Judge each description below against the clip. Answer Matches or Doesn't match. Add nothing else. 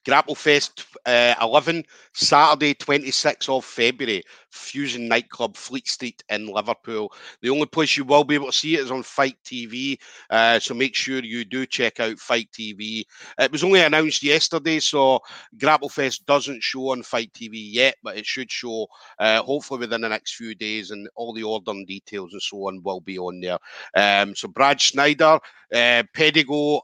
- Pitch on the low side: Matches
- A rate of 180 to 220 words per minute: Matches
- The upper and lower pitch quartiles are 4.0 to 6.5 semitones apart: Matches